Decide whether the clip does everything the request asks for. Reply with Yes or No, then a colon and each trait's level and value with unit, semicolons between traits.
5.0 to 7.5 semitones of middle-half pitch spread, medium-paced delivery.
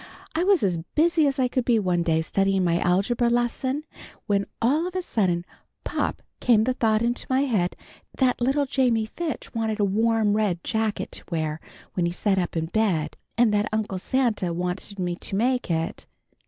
Yes: wide, 5.5 semitones; average, 190 wpm